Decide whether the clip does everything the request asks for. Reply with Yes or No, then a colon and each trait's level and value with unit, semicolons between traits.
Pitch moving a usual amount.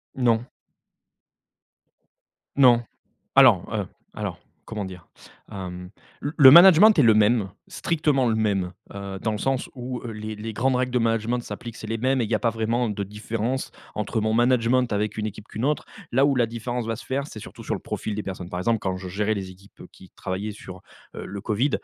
Yes: average, 3.3 semitones